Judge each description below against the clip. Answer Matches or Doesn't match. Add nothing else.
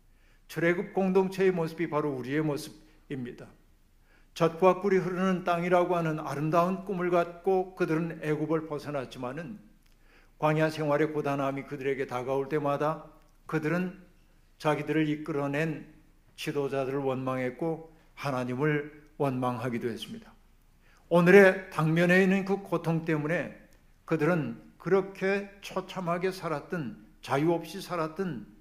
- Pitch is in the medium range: Matches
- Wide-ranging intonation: Doesn't match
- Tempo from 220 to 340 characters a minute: Matches